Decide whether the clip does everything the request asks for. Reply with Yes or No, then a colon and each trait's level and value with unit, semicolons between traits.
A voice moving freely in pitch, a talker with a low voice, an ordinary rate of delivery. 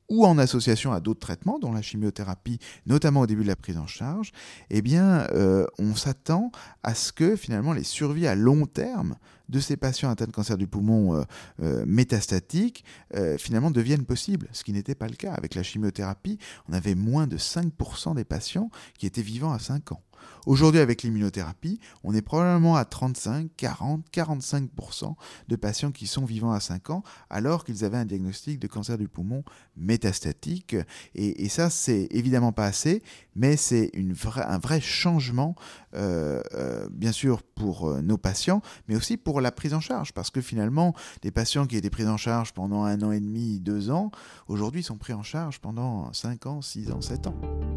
Yes: wide, 6.3 semitones; low, 115 Hz; average, 190 wpm